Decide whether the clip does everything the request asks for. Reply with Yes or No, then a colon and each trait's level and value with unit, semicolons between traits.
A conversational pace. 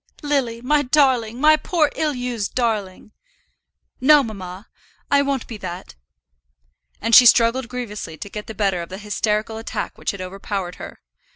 Yes: average, 160 wpm